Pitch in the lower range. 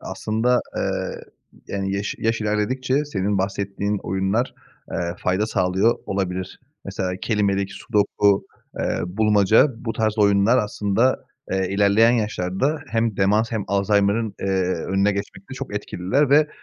Yes: low, 100 Hz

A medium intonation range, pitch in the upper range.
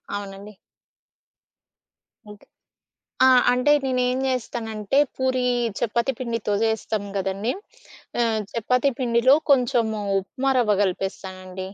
Yes: average, 3.7 semitones; high, 230 Hz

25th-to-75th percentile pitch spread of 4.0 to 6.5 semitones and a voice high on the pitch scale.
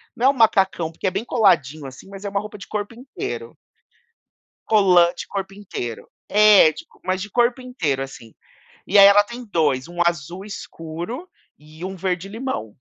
Yes: average, 4.4 semitones; high, 195 Hz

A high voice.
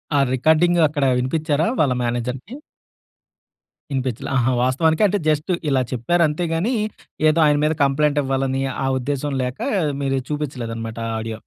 No: medium, 140 Hz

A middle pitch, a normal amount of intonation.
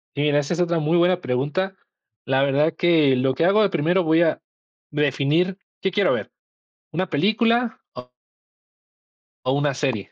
Yes: medium, 160 Hz; average, 4.5 semitones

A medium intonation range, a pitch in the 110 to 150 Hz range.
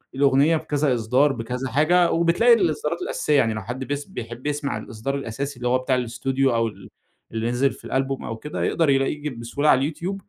Yes: average, 3.4 semitones; low, 135 Hz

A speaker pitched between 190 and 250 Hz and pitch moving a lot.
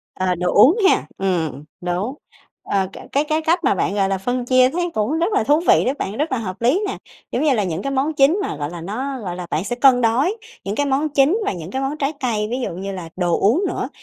Yes: high, 245 Hz; wide, 7.1 semitones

